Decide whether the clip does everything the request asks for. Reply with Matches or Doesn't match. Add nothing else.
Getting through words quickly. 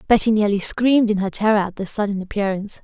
Matches